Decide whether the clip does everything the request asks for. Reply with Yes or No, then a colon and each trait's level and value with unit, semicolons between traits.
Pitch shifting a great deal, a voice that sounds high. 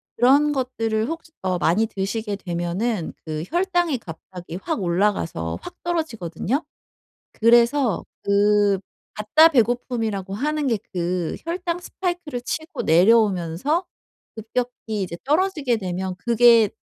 Yes: wide, 7.3 semitones; high, 225 Hz